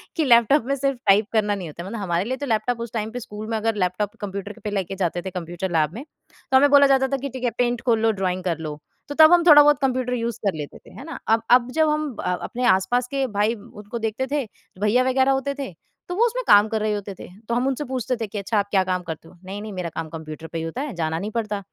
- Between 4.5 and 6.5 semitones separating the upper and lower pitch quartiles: Yes, wide, 5.4 semitones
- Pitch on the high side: Yes, high, 220 Hz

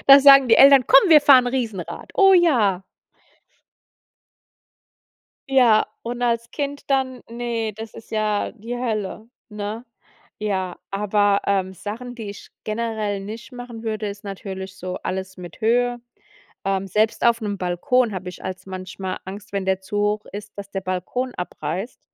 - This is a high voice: Yes, high, 215 Hz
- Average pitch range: Yes, average, 3.9 semitones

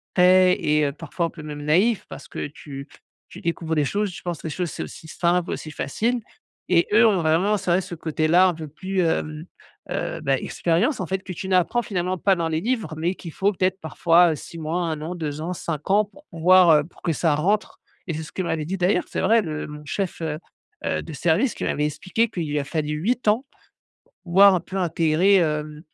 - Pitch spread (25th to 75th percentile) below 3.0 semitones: No, average, 3.4 semitones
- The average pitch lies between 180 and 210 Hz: No, medium, 170 Hz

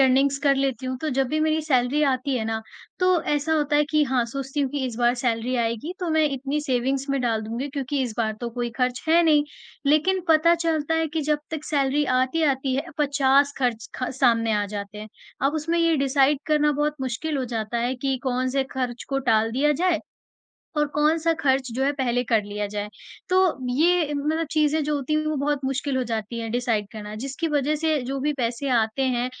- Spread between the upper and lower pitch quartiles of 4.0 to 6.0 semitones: No, average, 3.5 semitones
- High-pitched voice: Yes, very high, 270 Hz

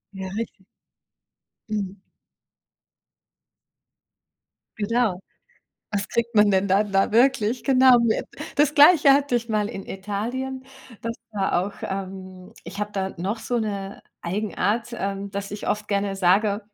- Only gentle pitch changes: No, average, 3.2 semitones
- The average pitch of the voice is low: No, high, 205 Hz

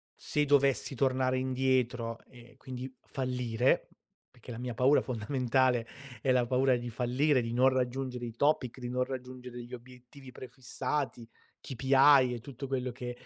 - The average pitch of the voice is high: No, low, 125 Hz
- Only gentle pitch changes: Yes, narrow, 1.4 semitones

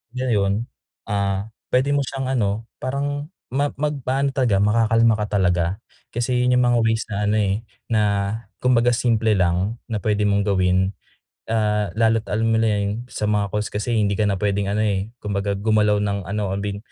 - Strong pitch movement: No, average, 3.0 semitones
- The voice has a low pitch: Yes, low, 105 Hz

